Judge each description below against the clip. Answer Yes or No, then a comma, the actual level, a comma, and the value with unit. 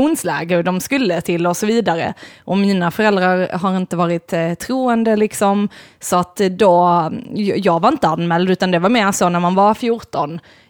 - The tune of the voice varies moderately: Yes, average, 3.5 semitones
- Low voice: No, medium, 185 Hz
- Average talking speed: Yes, average, 170 wpm